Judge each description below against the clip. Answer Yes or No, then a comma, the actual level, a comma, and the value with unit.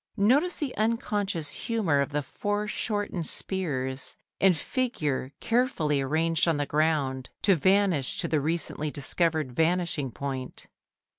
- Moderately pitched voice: Yes, medium, 165 Hz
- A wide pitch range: Yes, wide, 6.2 semitones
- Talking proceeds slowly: Yes, slow, 125 wpm